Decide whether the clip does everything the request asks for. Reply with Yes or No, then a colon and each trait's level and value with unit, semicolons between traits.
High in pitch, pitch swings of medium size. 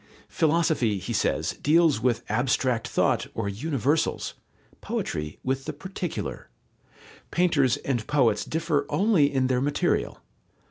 No: low, 135 Hz; average, 4.9 semitones